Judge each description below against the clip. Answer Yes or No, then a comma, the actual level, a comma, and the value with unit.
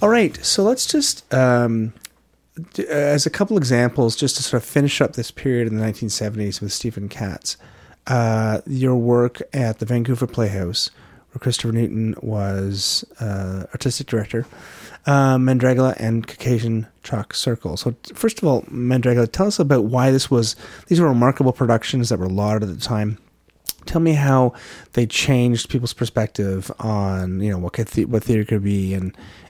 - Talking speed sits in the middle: Yes, average, 175 wpm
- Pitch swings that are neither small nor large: Yes, average, 3.5 semitones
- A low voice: Yes, low, 120 Hz